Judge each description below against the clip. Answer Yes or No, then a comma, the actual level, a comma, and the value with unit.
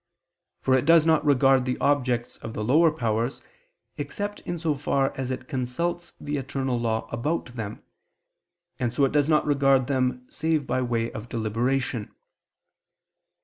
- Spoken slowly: No, average, 155 wpm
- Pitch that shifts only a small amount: No, average, 3.3 semitones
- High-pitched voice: No, low, 130 Hz